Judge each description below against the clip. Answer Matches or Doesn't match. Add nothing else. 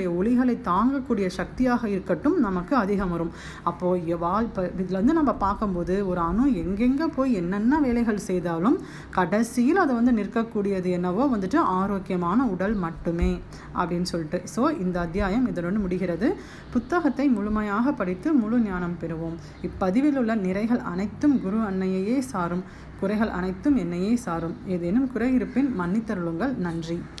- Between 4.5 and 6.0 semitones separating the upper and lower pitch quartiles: Matches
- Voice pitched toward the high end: Matches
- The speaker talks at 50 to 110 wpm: Doesn't match